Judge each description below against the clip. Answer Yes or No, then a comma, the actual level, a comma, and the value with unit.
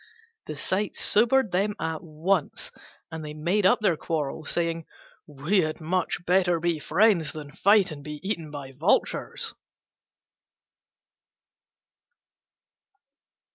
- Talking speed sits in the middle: No, slow, 115 wpm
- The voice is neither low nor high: Yes, medium, 170 Hz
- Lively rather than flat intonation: No, average, 4.0 semitones